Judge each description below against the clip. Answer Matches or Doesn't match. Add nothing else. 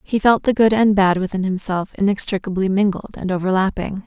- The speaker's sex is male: Doesn't match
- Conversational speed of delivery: Matches